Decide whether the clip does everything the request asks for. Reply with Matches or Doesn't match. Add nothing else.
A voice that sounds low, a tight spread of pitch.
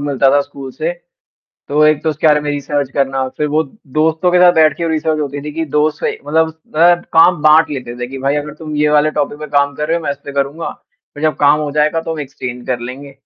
Doesn't match